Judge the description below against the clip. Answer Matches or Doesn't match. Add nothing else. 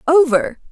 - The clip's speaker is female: Matches